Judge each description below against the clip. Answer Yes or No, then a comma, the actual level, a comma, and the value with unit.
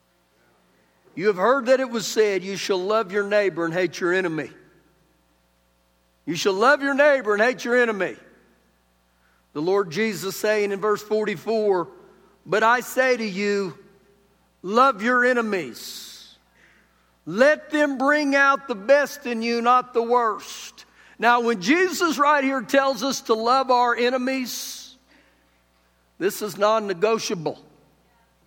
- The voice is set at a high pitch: Yes, high, 215 Hz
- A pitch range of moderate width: No, wide, 5.8 semitones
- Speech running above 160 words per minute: No, average, 140 wpm